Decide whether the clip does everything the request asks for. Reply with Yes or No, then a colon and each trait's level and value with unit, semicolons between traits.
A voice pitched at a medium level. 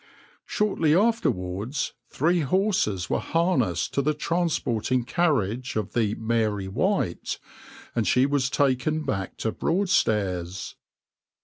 No: low, 130 Hz